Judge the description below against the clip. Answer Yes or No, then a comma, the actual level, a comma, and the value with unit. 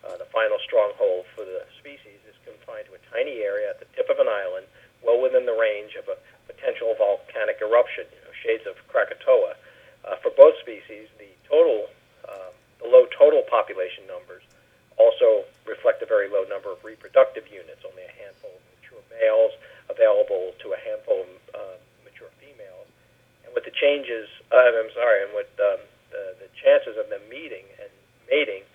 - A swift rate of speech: No, average, 180 wpm